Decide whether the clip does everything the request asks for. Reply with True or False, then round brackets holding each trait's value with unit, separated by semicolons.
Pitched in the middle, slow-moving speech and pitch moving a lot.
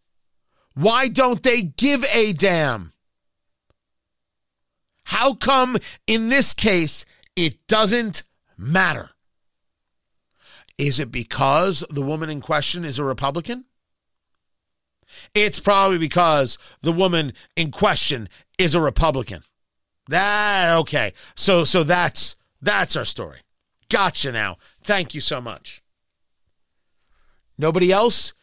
True (165 Hz; 105 wpm; 7.7 semitones)